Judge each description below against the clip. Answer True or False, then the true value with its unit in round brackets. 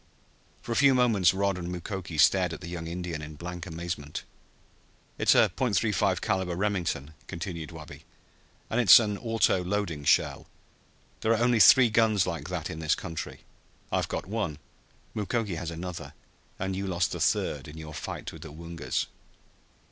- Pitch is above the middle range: False (90 Hz)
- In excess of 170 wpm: False (165 wpm)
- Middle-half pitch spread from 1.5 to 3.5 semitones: False (4.0 semitones)